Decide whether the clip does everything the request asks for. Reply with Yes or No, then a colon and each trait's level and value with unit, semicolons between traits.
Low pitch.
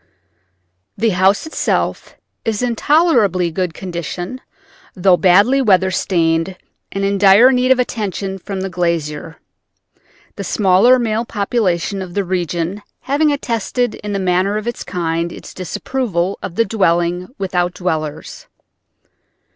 No: high, 190 Hz